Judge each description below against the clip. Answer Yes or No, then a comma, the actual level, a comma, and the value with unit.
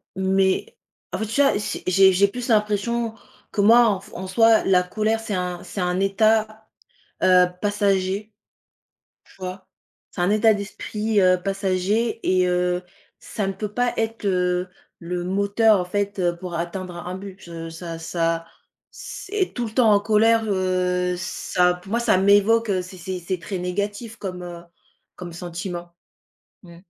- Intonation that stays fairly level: No, average, 3.1 semitones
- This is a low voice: No, high, 195 Hz